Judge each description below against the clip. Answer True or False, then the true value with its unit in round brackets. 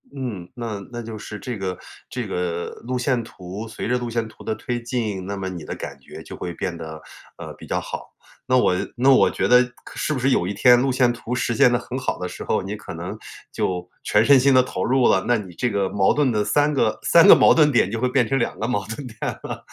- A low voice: True (115 Hz)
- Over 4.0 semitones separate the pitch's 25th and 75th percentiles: True (4.6 semitones)